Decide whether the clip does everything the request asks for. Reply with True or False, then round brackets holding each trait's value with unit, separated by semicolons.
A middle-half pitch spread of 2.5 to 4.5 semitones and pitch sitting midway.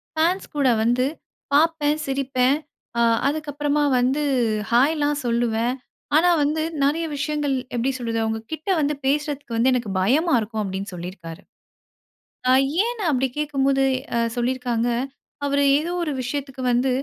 False (3.7 semitones; 270 Hz)